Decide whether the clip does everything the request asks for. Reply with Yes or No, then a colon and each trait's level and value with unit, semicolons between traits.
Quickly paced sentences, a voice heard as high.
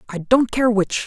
Yes: fast, 225 wpm; high, 225 Hz